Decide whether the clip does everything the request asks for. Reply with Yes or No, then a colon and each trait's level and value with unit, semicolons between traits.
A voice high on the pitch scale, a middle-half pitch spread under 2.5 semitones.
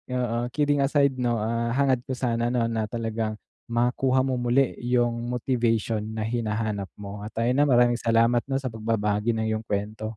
No: low, 115 Hz; narrow, 2.0 semitones